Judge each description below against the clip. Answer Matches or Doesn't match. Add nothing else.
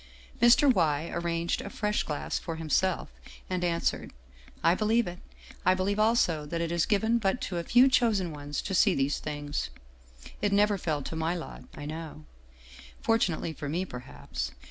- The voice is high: Doesn't match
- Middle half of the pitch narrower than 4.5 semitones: Doesn't match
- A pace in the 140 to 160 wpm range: Doesn't match